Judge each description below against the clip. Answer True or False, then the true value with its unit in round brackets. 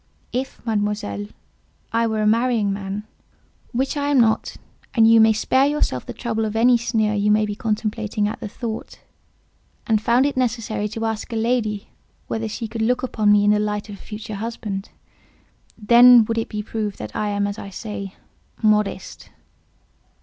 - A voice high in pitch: True (220 Hz)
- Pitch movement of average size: False (1.9 semitones)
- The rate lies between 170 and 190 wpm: True (180 wpm)